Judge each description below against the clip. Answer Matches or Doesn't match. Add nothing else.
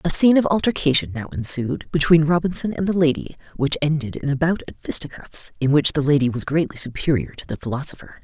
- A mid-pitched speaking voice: Matches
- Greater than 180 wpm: Matches